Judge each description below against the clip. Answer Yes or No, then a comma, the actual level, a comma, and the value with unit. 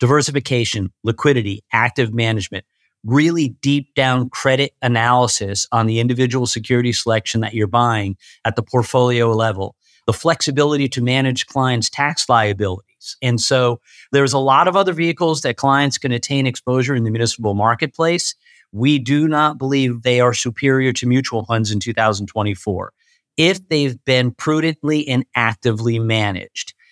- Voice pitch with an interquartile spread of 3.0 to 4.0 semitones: Yes, average, 3.5 semitones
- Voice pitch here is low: Yes, low, 125 Hz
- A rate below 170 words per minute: Yes, average, 145 wpm